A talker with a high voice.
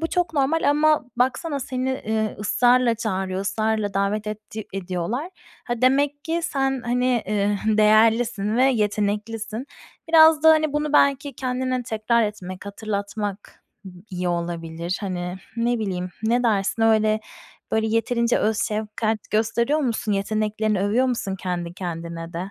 Yes: high, 220 Hz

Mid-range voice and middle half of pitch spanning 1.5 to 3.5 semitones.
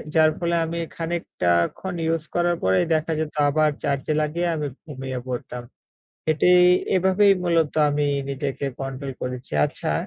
No: medium, 155 Hz; average, 4.0 semitones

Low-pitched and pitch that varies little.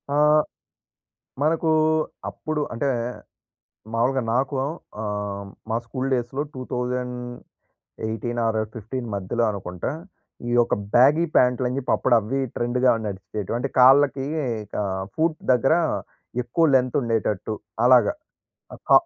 No: low, 125 Hz; average, 3.0 semitones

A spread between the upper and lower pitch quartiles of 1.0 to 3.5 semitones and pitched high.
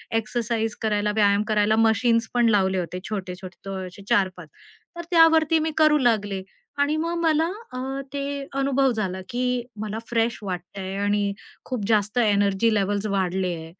No: average, 4.0 semitones; high, 215 Hz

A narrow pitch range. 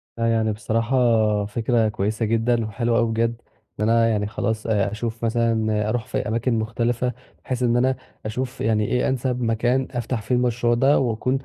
Yes: narrow, 1.8 semitones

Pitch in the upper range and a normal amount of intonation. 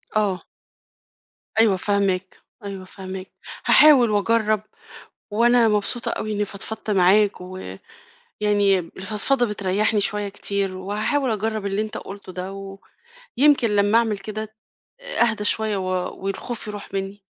No: high, 205 Hz; narrow, 2.0 semitones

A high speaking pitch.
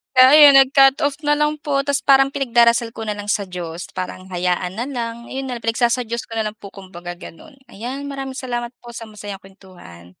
Yes: high, 235 Hz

